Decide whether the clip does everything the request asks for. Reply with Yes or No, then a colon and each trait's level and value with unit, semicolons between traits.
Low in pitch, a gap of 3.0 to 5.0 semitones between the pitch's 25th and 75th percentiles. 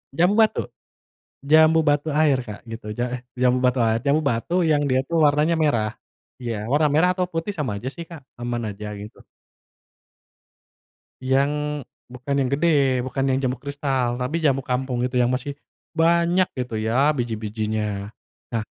Yes: low, 130 Hz; average, 3.9 semitones